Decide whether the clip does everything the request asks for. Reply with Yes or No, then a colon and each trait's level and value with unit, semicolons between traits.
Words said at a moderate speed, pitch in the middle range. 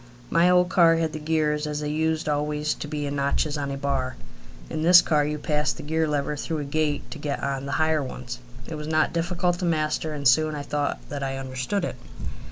No: fast, 230 wpm; medium, 150 Hz